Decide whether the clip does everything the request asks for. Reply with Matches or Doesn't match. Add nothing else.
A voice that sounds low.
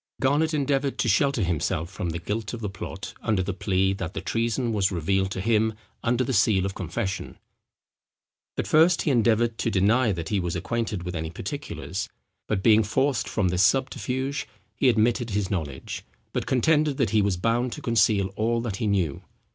Matches